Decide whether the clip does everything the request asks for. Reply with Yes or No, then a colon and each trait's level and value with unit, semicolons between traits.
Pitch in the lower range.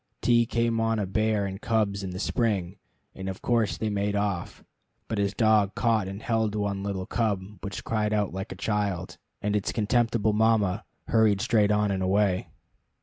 Yes: low, 105 Hz